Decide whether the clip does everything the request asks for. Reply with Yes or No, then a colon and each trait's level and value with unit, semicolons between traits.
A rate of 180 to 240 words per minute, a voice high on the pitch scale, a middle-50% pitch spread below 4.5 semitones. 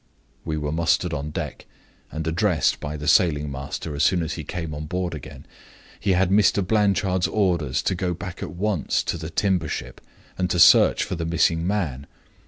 No: average, 190 wpm; very low, 85 Hz; average, 3.3 semitones